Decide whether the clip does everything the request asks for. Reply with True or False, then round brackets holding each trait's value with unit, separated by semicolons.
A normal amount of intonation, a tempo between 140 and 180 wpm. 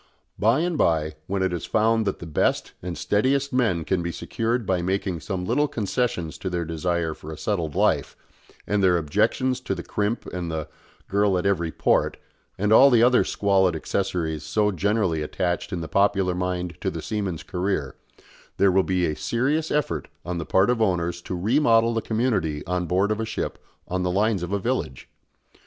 False (4.2 semitones; 195 wpm)